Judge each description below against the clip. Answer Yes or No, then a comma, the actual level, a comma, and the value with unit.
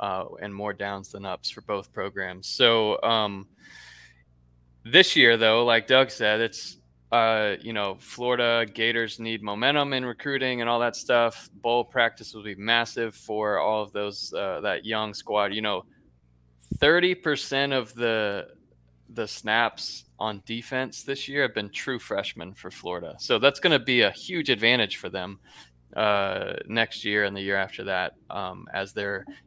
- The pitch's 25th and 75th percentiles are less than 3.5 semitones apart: Yes, average, 3.0 semitones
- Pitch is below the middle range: Yes, low, 110 Hz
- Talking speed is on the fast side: No, average, 170 wpm